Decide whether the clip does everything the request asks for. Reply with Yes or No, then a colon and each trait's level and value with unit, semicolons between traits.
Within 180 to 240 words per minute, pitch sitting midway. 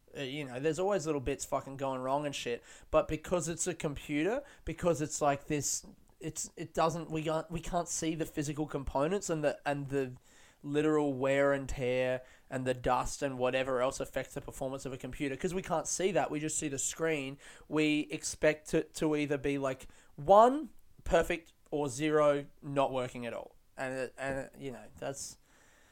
Yes: average, 195 wpm; medium, 145 Hz